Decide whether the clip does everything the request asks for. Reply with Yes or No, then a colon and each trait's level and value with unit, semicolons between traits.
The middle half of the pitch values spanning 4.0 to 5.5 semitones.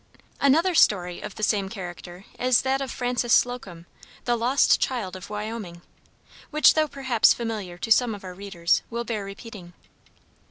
Yes: average, 4.7 semitones